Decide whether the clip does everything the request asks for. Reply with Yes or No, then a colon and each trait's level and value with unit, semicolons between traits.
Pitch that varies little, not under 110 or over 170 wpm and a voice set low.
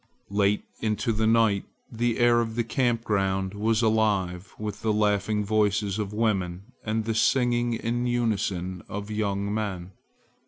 Yes: narrow, 2.3 semitones; average, 150 wpm; low, 105 Hz